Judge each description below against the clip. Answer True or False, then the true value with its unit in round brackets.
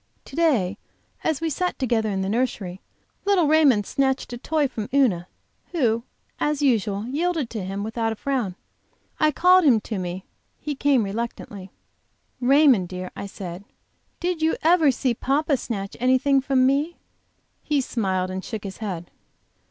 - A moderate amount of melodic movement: False (6.4 semitones)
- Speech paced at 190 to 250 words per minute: False (160 wpm)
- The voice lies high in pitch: True (250 Hz)